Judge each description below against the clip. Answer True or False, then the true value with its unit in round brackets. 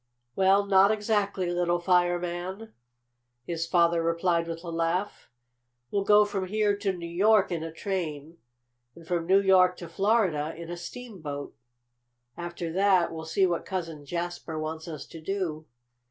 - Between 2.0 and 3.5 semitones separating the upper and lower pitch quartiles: True (2.7 semitones)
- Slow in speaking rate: False (155 wpm)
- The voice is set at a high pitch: False (175 Hz)